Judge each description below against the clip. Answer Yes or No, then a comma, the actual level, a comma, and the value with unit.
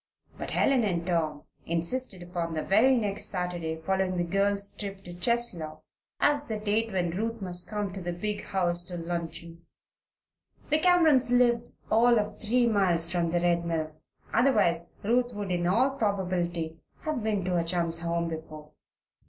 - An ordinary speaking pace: Yes, average, 165 wpm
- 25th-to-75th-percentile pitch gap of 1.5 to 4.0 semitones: No, average, 4.5 semitones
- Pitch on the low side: No, medium, 185 Hz